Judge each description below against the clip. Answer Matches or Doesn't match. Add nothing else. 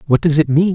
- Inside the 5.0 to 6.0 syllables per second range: Doesn't match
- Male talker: Matches